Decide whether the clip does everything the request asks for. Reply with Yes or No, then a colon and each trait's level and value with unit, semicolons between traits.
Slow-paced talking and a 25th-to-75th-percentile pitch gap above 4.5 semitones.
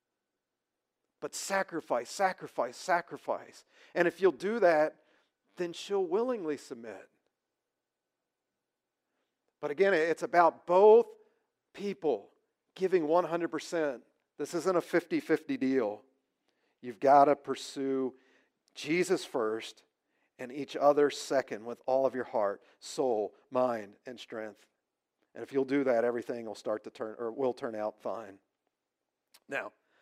Yes: slow, 120 wpm; wide, 5.6 semitones